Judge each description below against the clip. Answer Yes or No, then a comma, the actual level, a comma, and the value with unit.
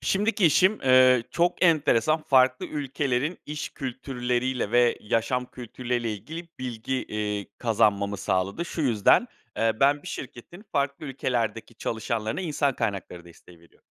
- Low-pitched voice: Yes, low, 125 Hz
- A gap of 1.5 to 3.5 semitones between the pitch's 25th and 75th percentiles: No, average, 4.4 semitones